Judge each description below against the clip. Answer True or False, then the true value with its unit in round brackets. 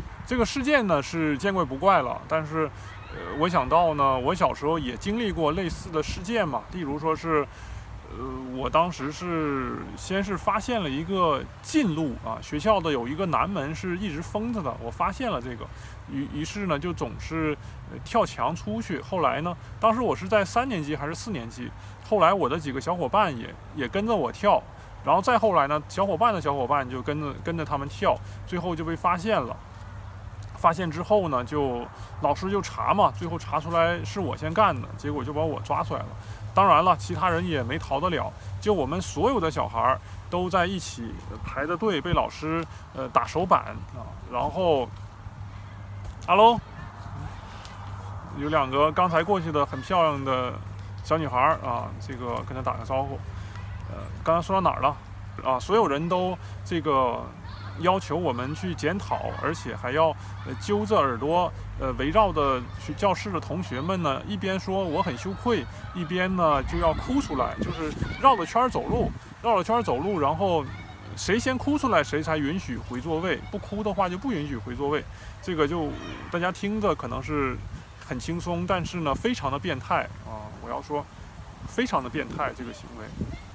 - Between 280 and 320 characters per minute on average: False (265 characters per minute)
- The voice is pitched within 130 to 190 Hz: True (140 Hz)